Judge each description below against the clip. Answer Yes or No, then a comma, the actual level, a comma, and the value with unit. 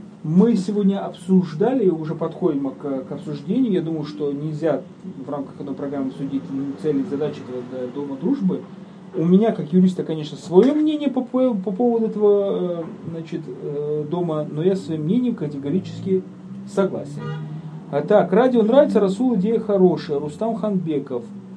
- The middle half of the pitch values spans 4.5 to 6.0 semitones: Yes, average, 5.1 semitones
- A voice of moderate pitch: Yes, medium, 180 Hz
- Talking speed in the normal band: Yes, average, 140 wpm